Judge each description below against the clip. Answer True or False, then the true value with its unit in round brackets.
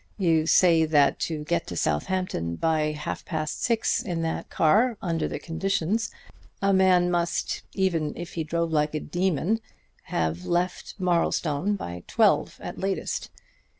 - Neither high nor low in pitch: True (170 Hz)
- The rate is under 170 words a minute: True (150 wpm)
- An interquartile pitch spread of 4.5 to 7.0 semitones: False (3.5 semitones)